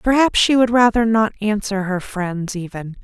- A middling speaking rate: Yes, average, 180 wpm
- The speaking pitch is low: No, high, 210 Hz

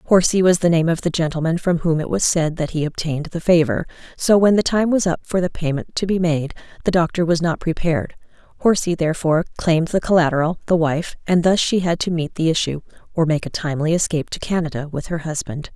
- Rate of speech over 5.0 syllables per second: Yes, 6.2 syllables/s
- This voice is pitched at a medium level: Yes, medium, 165 Hz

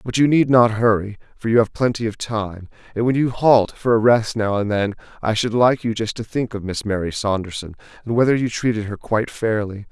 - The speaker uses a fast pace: Yes, fast, 235 wpm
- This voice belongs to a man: Yes, male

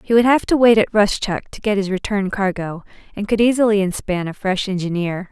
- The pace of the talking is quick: Yes, fast, 215 wpm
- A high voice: Yes, high, 200 Hz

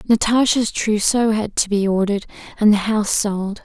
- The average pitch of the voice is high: Yes, high, 210 Hz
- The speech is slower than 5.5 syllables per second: Yes, 5.2 syllables/s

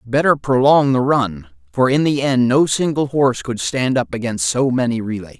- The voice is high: No, low, 125 Hz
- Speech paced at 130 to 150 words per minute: No, average, 200 wpm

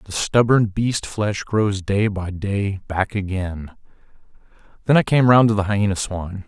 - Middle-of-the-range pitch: No, low, 100 Hz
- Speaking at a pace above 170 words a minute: No, average, 165 wpm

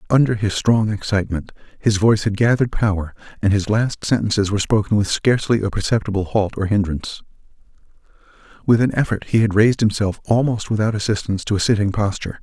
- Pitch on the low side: Yes, low, 105 Hz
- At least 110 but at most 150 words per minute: No, average, 175 wpm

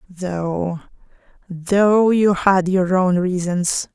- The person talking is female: Yes, female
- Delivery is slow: Yes, slow, 105 wpm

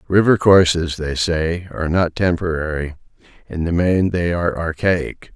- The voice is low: Yes, very low, 85 Hz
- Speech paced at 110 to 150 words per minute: Yes, slow, 135 wpm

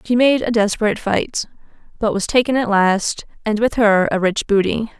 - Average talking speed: Yes, average, 190 wpm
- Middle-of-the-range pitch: No, high, 215 Hz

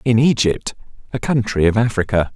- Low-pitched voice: Yes, low, 110 Hz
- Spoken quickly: No, average, 155 wpm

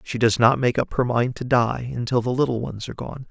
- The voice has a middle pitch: No, low, 120 Hz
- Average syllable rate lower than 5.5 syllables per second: No, 5.7 syllables/s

